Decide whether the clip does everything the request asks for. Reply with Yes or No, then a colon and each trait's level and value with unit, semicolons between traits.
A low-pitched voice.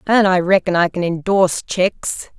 No: medium, 185 Hz